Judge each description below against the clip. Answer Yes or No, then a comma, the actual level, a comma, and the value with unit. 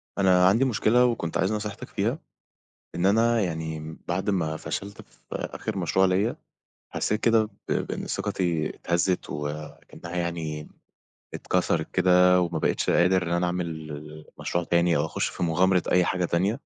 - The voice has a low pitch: Yes, very low, 90 Hz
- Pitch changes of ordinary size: Yes, average, 3.0 semitones